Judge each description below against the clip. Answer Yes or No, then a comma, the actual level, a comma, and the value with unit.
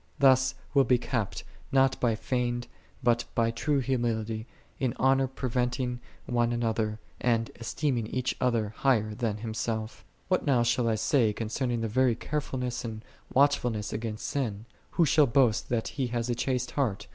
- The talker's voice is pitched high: No, low, 120 Hz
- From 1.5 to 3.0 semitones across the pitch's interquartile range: Yes, narrow, 2.6 semitones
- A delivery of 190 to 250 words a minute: No, average, 180 wpm